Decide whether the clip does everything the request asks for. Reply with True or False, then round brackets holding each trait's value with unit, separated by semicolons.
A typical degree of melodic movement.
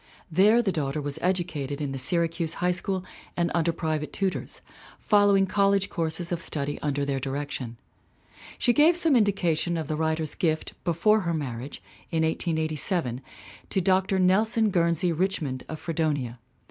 True (4.1 semitones)